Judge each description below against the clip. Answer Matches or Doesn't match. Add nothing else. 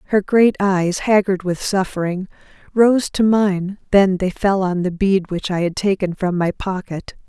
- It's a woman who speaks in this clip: Matches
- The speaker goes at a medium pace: Matches